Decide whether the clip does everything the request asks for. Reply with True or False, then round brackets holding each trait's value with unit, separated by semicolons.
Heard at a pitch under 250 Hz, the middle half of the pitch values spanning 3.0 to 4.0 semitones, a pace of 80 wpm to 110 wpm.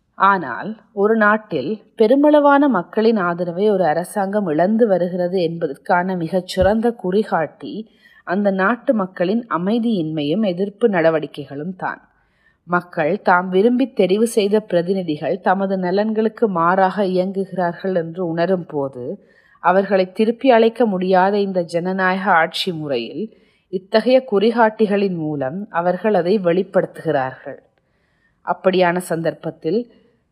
True (190 Hz; 3.6 semitones; 95 wpm)